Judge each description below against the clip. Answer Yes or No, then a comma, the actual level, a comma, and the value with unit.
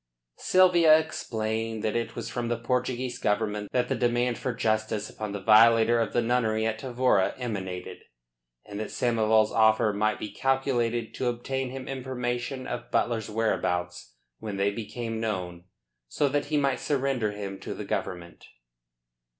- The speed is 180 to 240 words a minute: No, average, 155 wpm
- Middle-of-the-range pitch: No, low, 115 Hz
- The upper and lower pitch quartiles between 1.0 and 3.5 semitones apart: Yes, average, 2.7 semitones